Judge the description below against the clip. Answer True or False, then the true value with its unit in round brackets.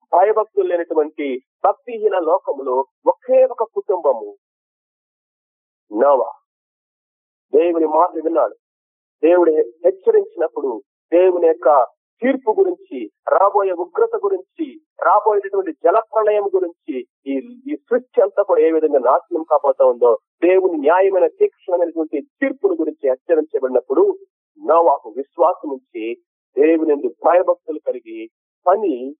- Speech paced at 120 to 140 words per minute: False (90 wpm)